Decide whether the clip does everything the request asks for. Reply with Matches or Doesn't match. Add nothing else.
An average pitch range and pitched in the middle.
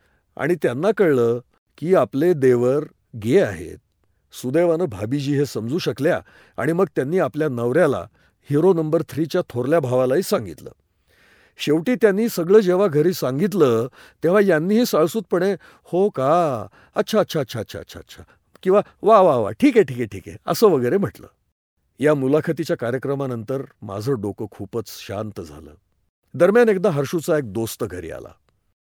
Doesn't match